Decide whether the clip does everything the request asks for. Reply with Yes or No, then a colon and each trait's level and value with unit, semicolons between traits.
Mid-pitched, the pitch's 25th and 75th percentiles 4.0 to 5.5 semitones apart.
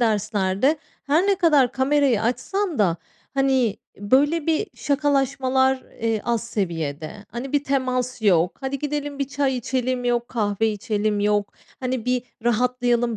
No: very high, 250 Hz; average, 4.3 semitones